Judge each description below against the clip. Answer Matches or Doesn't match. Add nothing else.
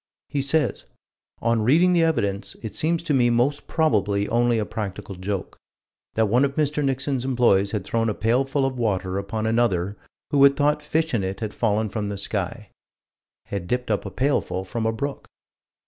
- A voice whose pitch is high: Doesn't match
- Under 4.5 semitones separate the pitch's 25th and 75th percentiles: Doesn't match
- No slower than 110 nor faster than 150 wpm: Doesn't match